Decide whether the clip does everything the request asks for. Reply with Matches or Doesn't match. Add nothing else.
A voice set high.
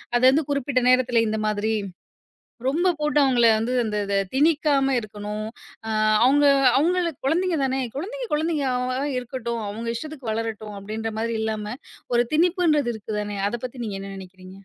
Matches